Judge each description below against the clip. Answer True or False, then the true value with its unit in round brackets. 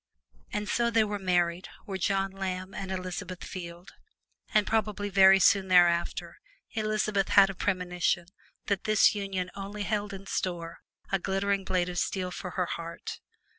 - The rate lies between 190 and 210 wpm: False (155 wpm)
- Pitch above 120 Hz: True (190 Hz)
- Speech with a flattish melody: True (1.9 semitones)